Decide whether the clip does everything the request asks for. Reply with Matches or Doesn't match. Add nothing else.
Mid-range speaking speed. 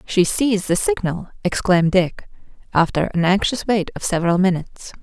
Matches